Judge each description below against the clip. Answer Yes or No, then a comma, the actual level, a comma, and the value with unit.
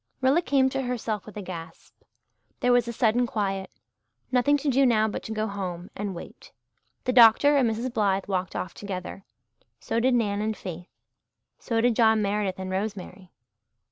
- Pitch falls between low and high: No, high, 215 Hz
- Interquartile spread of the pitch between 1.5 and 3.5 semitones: No, average, 4.0 semitones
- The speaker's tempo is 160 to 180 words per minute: Yes, average, 175 wpm